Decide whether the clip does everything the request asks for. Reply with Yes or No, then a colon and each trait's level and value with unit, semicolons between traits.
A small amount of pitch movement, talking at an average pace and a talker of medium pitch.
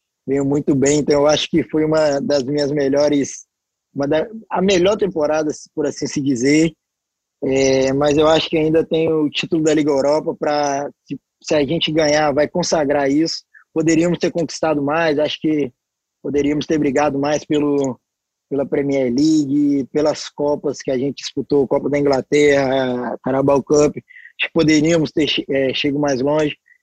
Yes: narrow, 2.1 semitones; average, 160 wpm; medium, 150 Hz